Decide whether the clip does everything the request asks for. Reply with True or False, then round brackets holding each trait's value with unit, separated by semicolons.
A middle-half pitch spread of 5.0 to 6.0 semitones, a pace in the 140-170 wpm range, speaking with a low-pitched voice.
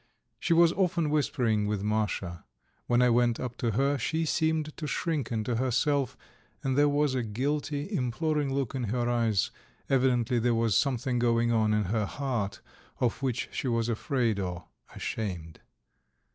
False (4.3 semitones; 160 wpm; 125 Hz)